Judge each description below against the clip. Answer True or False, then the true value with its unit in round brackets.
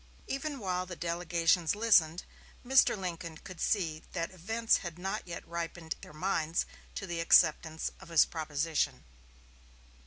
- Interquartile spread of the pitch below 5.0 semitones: True (2.9 semitones)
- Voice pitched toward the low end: False (170 Hz)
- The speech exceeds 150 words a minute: False (135 wpm)